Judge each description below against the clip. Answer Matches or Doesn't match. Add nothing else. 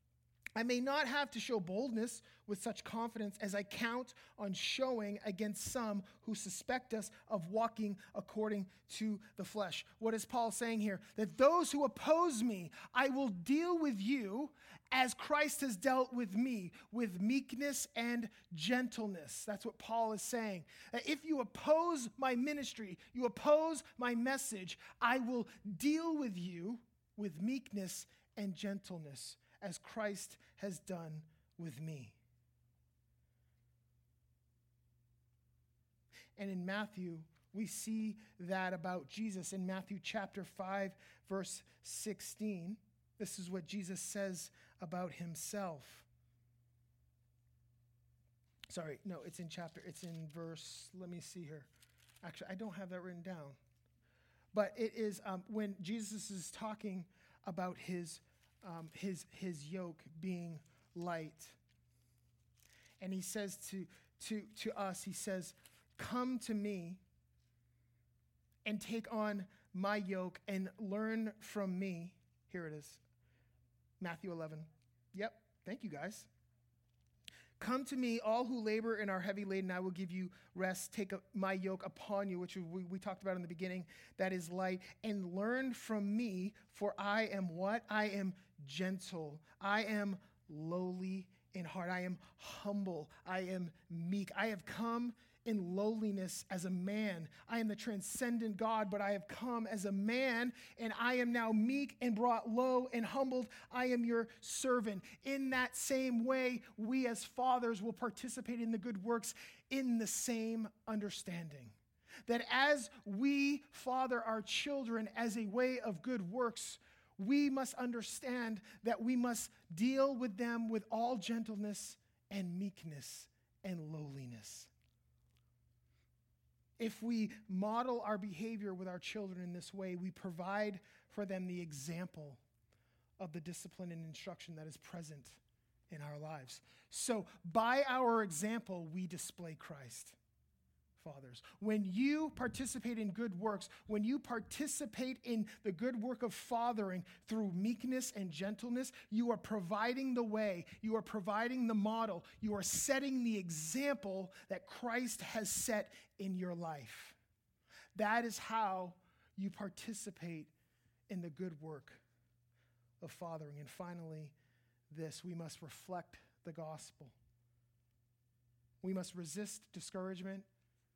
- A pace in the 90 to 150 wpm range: Matches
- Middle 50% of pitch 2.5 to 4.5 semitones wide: Doesn't match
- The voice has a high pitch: Matches